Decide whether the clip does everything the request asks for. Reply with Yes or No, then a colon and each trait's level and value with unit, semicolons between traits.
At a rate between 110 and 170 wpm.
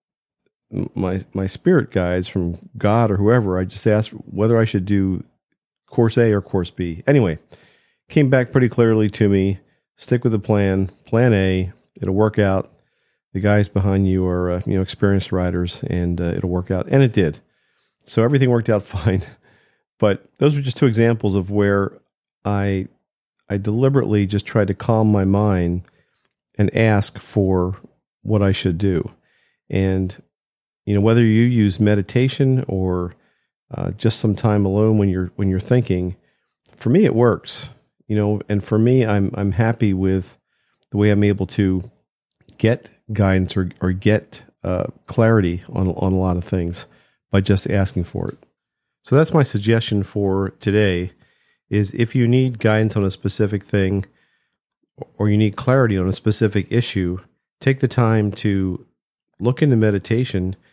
Yes: average, 165 wpm